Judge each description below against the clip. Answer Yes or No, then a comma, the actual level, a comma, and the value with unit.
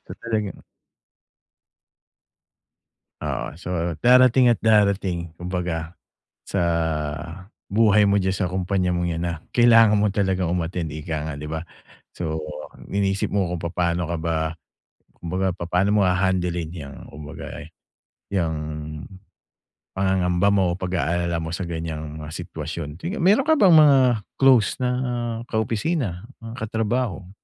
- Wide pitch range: No, average, 3.8 semitones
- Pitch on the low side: Yes, very low, 90 Hz